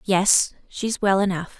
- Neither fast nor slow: Yes, average, 150 wpm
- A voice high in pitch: Yes, high, 195 Hz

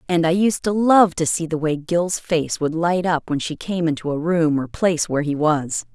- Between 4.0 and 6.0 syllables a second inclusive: Yes, 4.9 syllables/s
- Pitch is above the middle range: No, medium, 165 Hz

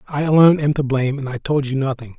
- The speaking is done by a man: Yes, male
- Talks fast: Yes, fast, 275 wpm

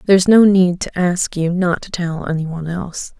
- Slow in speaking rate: No, fast, 205 wpm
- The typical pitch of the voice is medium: Yes, medium, 175 Hz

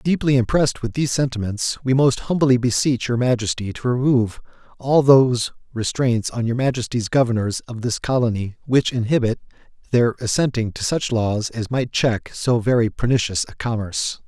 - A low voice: Yes, low, 120 Hz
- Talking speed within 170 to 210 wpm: No, average, 160 wpm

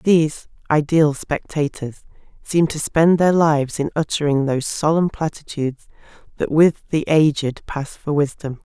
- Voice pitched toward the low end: No, medium, 150 Hz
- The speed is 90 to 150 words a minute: Yes, average, 140 wpm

